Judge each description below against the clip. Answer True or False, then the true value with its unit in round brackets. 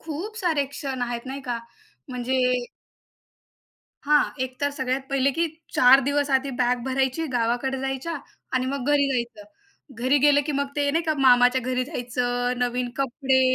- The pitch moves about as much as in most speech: False (2.3 semitones)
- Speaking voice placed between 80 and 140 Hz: False (265 Hz)